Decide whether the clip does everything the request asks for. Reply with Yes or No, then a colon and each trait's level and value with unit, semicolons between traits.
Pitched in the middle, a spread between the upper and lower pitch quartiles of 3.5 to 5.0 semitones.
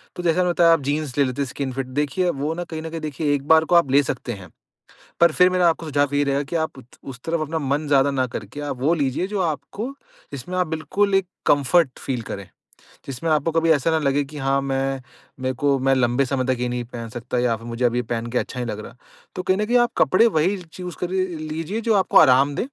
Yes: medium, 145 Hz; average, 4.1 semitones